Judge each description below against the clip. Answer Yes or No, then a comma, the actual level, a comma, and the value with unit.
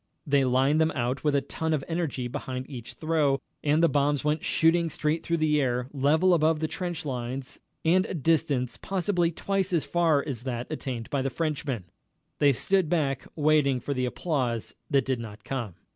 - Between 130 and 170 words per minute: No, average, 190 wpm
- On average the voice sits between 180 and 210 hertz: No, medium, 145 Hz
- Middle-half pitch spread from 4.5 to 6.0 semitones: No, average, 3.8 semitones